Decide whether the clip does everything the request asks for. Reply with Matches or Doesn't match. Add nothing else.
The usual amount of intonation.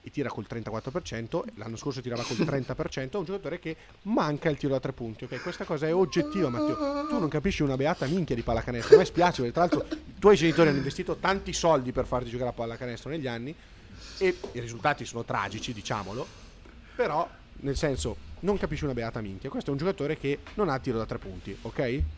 Doesn't match